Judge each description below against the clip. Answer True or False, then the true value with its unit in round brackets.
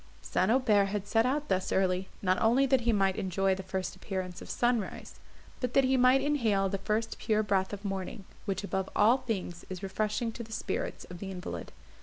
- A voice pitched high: True (205 Hz)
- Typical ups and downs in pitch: True (3.8 semitones)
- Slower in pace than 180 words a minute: False (205 wpm)